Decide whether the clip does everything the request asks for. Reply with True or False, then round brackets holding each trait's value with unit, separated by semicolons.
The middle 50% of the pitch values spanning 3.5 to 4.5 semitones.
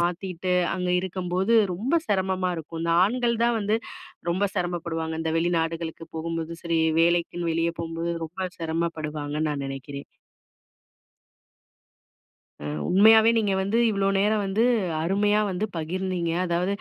False (2.9 semitones)